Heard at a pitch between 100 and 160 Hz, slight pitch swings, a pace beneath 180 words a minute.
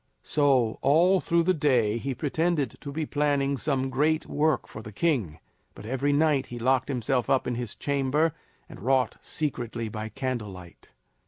No: low, 135 Hz; average, 3.8 semitones; average, 170 wpm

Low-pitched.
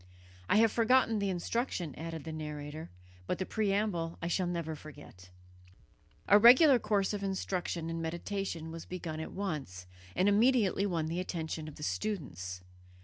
No: medium, 175 Hz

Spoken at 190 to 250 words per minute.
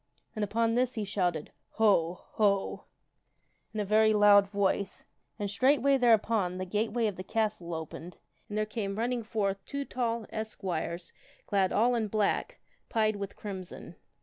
No: average, 165 wpm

